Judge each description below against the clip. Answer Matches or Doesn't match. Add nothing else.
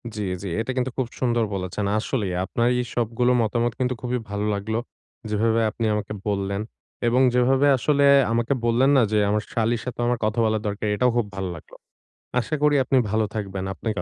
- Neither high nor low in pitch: Doesn't match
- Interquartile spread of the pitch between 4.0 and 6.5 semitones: Doesn't match